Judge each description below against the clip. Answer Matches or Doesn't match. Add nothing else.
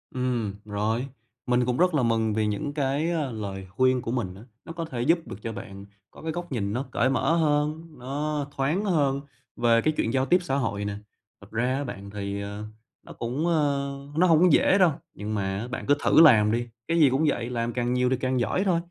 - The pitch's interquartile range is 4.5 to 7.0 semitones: Matches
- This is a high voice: Doesn't match